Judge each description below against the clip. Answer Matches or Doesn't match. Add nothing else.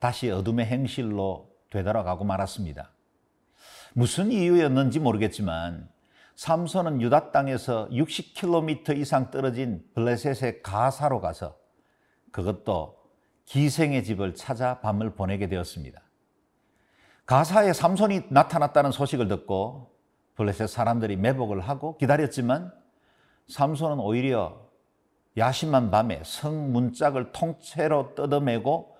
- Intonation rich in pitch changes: Matches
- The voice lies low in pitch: Matches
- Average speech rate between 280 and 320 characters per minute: Doesn't match